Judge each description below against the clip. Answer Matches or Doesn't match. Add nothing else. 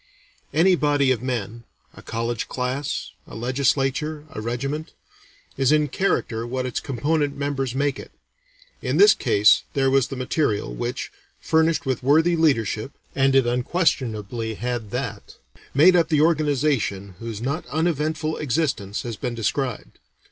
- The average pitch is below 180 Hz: Matches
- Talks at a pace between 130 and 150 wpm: Matches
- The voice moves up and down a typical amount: Matches